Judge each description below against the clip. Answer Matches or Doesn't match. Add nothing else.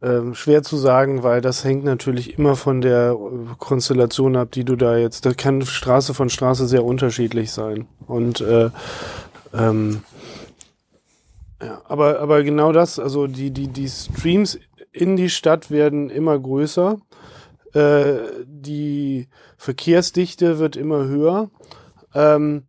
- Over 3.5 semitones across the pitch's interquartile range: Doesn't match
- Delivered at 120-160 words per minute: Matches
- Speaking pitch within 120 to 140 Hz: Matches